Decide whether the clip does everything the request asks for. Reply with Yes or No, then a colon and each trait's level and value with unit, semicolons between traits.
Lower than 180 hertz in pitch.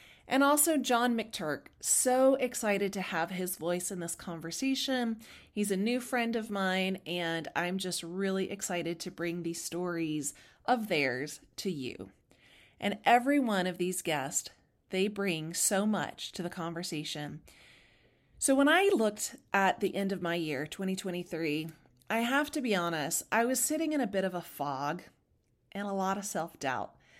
No: high, 190 Hz